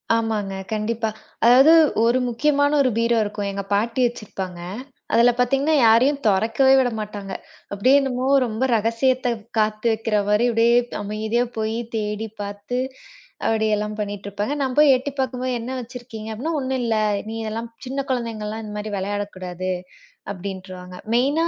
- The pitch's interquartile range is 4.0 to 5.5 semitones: No, average, 3.2 semitones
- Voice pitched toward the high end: Yes, high, 225 Hz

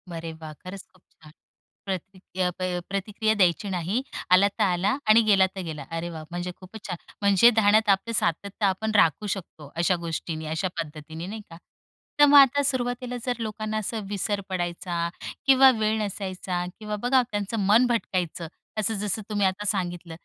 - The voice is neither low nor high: No, high, 195 Hz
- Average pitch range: Yes, average, 3.6 semitones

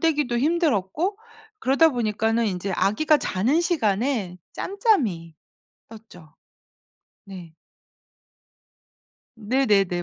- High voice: Yes, high, 225 Hz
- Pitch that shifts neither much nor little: No, wide, 7.6 semitones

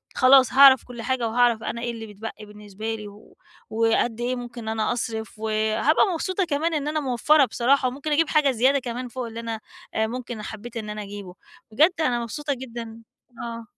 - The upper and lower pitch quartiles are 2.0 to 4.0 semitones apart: Yes, average, 3.0 semitones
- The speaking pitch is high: Yes, high, 235 Hz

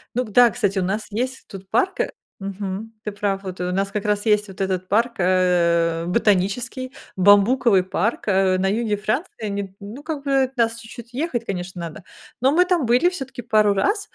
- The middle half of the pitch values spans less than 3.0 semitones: No, average, 4.3 semitones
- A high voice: Yes, high, 210 Hz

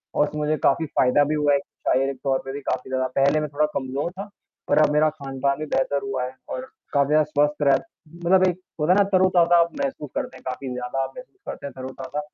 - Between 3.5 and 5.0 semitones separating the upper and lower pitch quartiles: No, narrow, 2.5 semitones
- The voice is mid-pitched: Yes, medium, 145 Hz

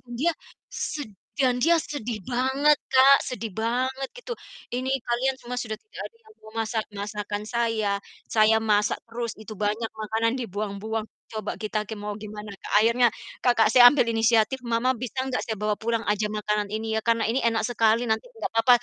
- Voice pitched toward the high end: Yes, high, 225 Hz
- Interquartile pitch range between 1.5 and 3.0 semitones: Yes, narrow, 2.6 semitones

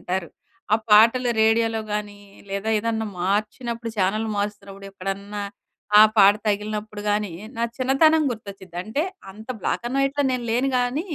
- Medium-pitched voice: No, high, 215 Hz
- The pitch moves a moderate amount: Yes, average, 3.0 semitones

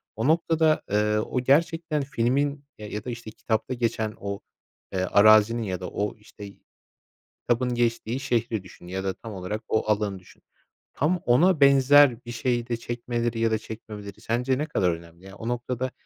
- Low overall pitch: Yes, low, 115 Hz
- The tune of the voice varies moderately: Yes, average, 3.5 semitones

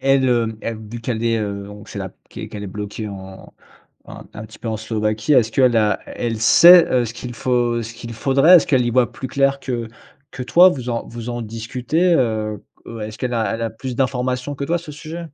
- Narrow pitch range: No, average, 3.2 semitones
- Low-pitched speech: Yes, low, 120 Hz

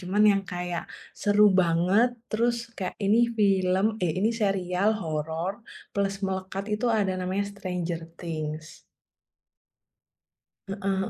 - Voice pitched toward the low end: No, high, 190 Hz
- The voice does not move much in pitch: Yes, narrow, 2.2 semitones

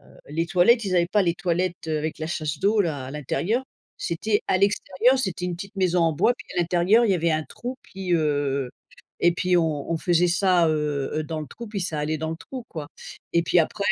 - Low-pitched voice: No, medium, 170 Hz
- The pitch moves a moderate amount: Yes, average, 3.5 semitones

